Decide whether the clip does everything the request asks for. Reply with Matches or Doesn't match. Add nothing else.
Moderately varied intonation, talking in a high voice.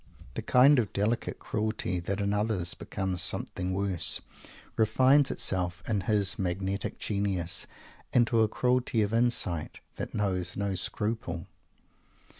Doesn't match